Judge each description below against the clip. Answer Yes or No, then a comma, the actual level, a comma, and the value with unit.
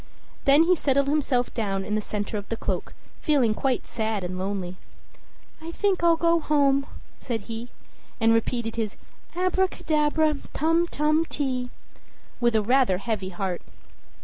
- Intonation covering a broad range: Yes, wide, 6.2 semitones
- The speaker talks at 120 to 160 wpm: Yes, average, 150 wpm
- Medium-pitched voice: No, very high, 250 Hz